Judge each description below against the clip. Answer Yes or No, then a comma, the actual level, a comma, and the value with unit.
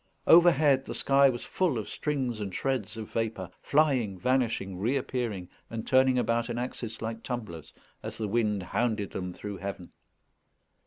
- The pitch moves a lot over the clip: No, average, 4.2 semitones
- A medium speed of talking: Yes, average, 155 wpm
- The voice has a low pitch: Yes, low, 115 Hz